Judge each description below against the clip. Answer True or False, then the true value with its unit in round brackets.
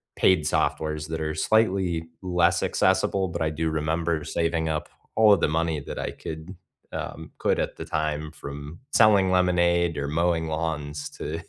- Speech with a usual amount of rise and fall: False (2.2 semitones)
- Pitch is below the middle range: True (80 Hz)